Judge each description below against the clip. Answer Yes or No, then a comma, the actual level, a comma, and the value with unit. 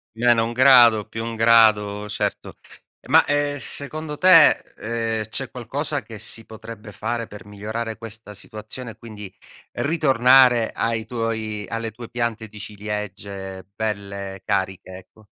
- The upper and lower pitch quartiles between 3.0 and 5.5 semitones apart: No, narrow, 2.4 semitones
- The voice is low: Yes, low, 115 Hz